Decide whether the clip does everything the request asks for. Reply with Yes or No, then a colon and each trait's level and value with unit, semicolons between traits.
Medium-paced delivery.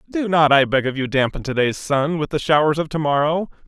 No: fast, 230 wpm